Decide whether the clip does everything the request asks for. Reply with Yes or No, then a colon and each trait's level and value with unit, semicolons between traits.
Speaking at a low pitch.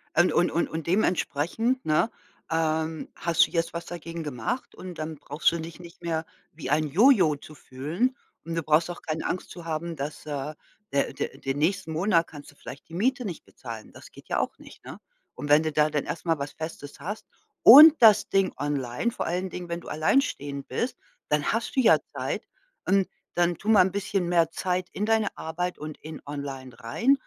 No: medium, 165 Hz